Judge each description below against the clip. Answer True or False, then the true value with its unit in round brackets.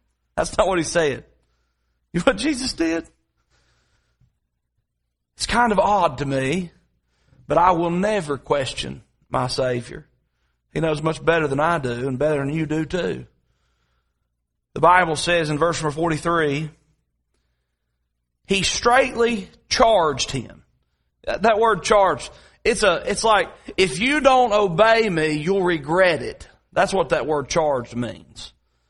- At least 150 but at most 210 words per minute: False (140 wpm)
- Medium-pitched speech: True (150 Hz)